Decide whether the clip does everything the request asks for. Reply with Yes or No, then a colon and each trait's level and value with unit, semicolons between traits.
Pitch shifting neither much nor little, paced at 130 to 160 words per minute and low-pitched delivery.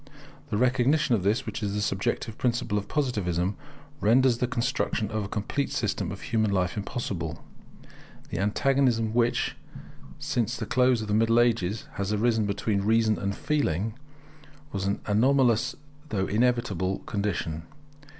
Yes: average, 3.4 semitones; average, 145 wpm; low, 110 Hz